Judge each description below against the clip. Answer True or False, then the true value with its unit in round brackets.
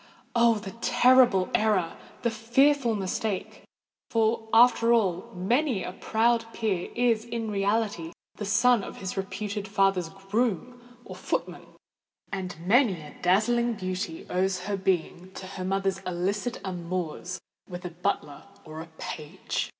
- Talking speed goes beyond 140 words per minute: False (135 wpm)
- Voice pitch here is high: True (195 Hz)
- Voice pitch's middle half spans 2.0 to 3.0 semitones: False (3.9 semitones)